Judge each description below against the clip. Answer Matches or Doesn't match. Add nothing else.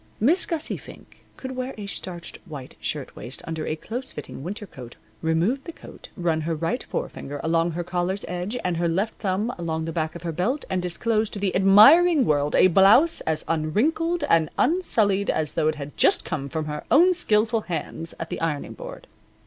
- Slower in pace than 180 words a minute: Doesn't match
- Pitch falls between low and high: Matches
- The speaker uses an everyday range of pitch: Doesn't match